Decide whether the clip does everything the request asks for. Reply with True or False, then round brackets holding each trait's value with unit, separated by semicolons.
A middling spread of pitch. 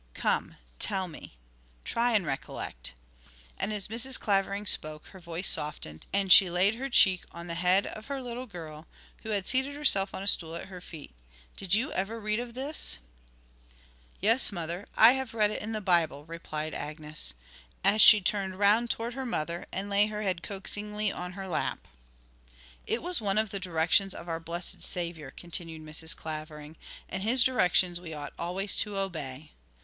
True (4.3 semitones)